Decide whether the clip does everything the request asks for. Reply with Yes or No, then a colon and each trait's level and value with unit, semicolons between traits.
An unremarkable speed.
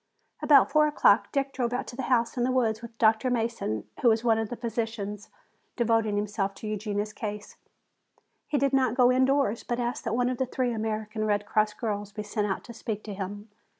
No: fast, 215 wpm